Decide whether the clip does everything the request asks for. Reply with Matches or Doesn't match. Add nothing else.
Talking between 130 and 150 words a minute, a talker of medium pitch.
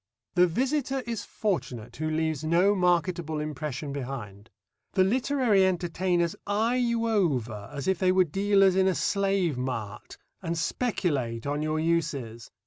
Matches